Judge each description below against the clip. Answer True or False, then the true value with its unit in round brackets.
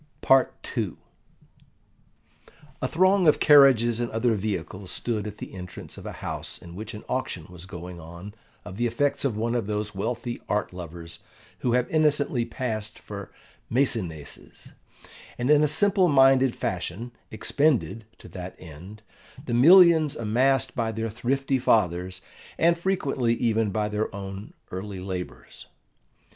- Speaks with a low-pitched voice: True (115 Hz)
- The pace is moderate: True (145 wpm)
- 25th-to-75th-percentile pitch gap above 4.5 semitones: True (5.6 semitones)